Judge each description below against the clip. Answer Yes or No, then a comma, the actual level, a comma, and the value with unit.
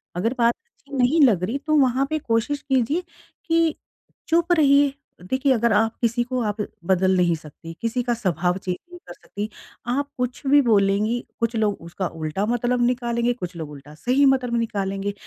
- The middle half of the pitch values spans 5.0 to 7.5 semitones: Yes, average, 5.3 semitones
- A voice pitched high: Yes, high, 235 Hz